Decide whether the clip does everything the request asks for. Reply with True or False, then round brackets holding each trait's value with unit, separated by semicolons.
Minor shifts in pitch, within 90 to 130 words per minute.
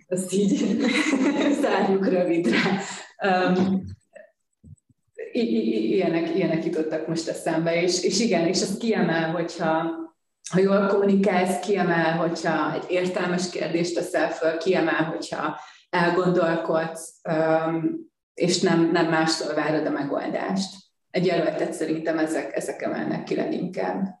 False (3.0 semitones; 120 wpm)